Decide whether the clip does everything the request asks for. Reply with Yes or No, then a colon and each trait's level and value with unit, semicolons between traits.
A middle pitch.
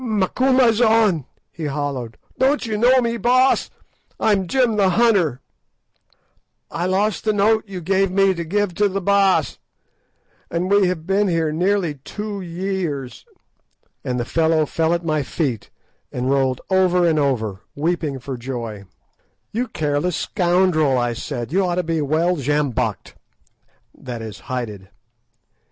Yes: medium, 175 Hz